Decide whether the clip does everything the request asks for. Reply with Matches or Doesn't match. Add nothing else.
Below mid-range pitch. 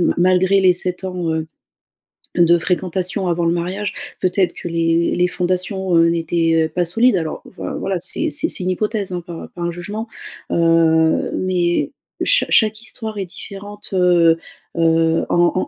Doesn't match